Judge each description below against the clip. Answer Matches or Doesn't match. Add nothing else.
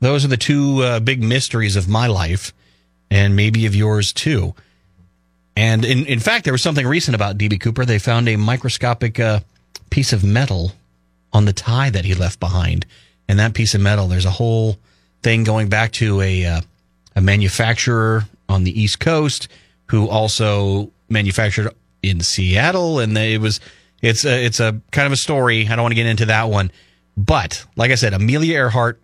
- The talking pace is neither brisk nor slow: Matches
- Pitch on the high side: Doesn't match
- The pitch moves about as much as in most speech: Matches